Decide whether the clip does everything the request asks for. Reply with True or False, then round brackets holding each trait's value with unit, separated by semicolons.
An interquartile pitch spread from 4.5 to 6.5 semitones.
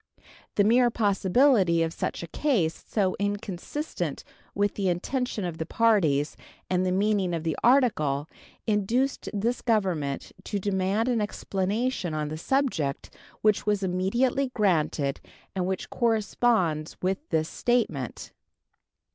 True (5.3 semitones)